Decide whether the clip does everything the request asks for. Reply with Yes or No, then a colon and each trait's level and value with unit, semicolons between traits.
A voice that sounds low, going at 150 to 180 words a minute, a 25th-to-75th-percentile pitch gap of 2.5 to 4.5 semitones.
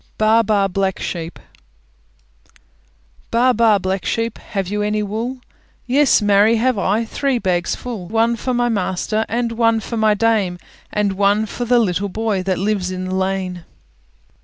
No: high, 210 Hz; average, 160 wpm; average, 3.1 semitones